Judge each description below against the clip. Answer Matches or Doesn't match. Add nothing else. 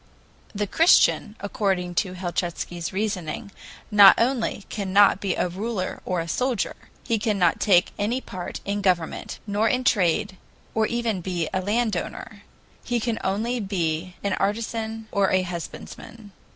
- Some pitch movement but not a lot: Matches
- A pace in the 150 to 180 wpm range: Doesn't match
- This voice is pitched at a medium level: Doesn't match